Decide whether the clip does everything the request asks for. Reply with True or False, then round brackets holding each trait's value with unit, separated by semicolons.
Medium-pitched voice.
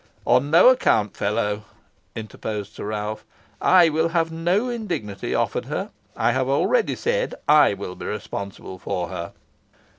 False (125 Hz)